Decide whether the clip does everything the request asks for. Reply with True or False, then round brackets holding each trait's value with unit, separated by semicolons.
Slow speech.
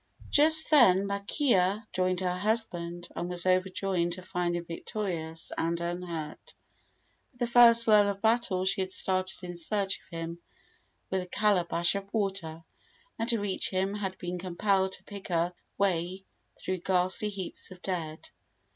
False (155 wpm)